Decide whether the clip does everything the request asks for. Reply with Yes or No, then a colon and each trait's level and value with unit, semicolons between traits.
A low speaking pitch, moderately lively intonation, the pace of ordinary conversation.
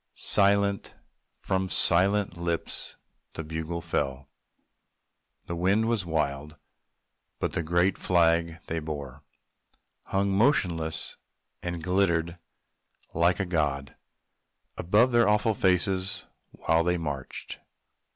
No: very low, 85 Hz; average, 3.3 semitones; slow, 100 wpm